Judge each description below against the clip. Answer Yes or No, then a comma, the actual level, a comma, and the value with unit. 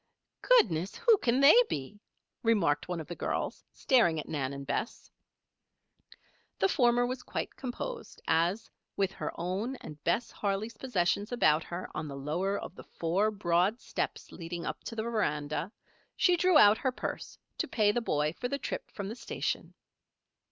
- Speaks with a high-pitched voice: Yes, high, 200 Hz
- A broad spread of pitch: Yes, wide, 6.4 semitones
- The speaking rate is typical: Yes, average, 170 wpm